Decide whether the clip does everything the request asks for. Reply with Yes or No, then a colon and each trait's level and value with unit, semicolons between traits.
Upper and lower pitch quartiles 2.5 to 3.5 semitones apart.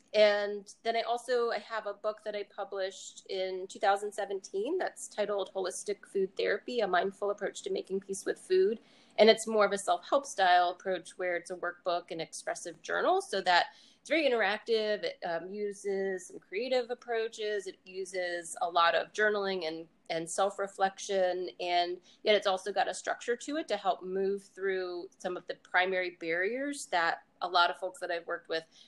No: average, 3.9 semitones